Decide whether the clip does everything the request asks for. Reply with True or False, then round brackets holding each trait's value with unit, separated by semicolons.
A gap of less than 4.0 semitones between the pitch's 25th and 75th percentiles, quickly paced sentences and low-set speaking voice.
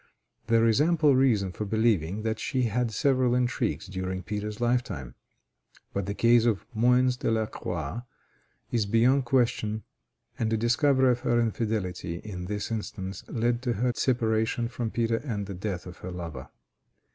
False (3.4 semitones; 160 wpm; 115 Hz)